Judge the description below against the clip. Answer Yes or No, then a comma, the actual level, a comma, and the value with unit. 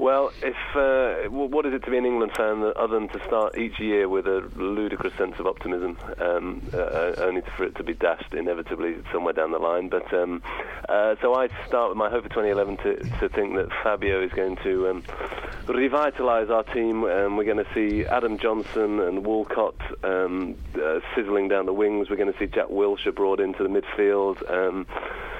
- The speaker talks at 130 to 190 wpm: No, fast, 205 wpm